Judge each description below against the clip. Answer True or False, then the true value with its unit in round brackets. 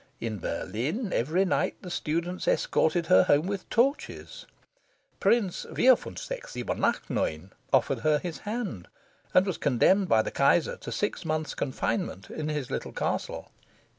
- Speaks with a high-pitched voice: False (175 Hz)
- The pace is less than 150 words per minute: True (135 wpm)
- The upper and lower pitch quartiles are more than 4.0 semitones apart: True (5.6 semitones)